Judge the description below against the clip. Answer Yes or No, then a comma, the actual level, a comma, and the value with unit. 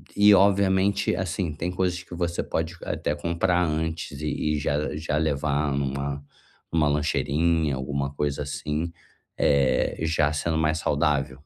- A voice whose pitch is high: No, very low, 75 Hz